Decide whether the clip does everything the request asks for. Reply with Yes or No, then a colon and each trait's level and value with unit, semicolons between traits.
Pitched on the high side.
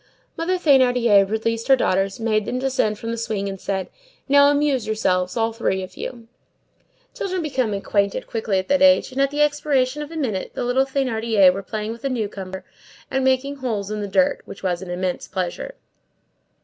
Yes: high, 230 Hz